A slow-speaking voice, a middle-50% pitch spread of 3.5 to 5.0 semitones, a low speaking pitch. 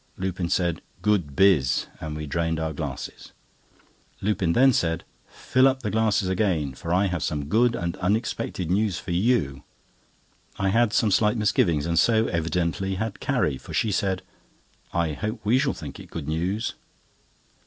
No: average, 165 wpm; average, 4.7 semitones; very low, 95 Hz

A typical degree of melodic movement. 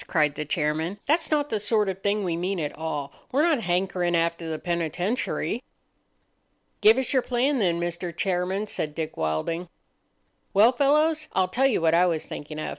No: wide, 5.9 semitones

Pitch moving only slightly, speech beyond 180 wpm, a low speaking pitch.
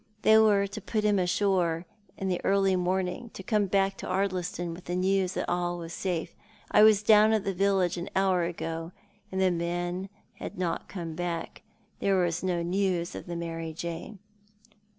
No: narrow, 2.2 semitones; average, 190 wpm; medium, 185 Hz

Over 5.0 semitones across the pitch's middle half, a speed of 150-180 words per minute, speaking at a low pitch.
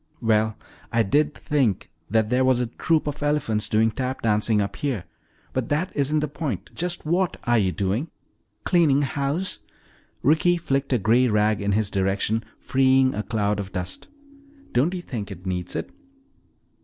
Yes: wide, 5.6 semitones; average, 170 wpm; low, 120 Hz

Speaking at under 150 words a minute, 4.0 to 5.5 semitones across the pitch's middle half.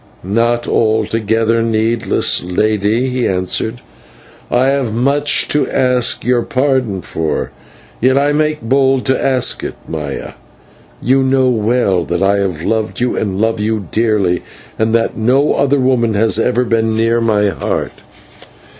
No: average, 140 wpm; average, 3.2 semitones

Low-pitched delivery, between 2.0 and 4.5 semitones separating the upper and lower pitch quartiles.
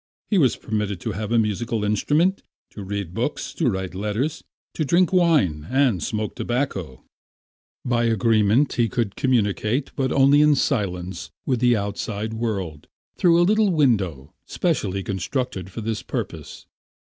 No: low, 110 Hz; wide, 5.4 semitones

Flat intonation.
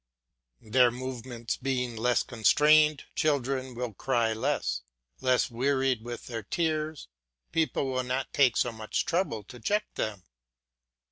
No: average, 3.0 semitones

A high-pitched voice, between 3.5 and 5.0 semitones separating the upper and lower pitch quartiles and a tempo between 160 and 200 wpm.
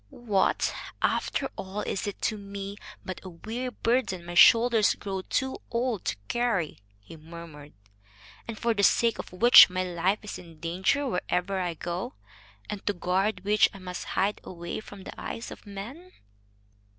Yes: high, 195 Hz; average, 3.9 semitones; average, 165 wpm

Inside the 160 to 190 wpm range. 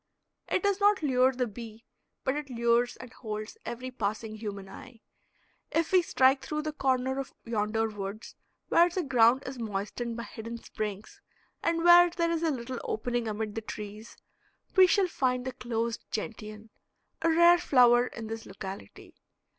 Yes: average, 165 wpm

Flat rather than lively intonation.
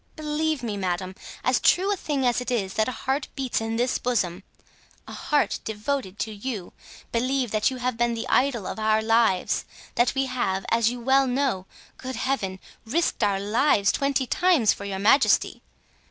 No: average, 4.3 semitones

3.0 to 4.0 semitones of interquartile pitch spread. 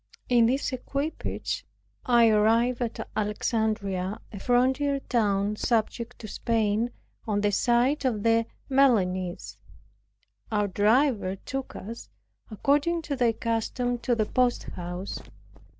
Yes: average, 3.3 semitones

